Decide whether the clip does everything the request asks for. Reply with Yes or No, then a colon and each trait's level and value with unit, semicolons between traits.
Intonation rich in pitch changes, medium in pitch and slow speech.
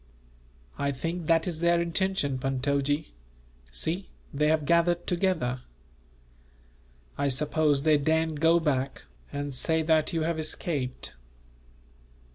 No: average, 3.0 semitones; medium, 155 Hz; slow, 115 wpm